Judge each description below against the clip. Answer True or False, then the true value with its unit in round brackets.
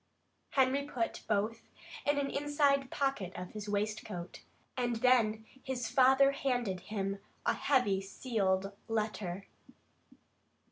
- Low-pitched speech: False (225 Hz)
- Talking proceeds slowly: True (110 wpm)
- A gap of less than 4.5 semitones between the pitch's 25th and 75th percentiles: False (4.9 semitones)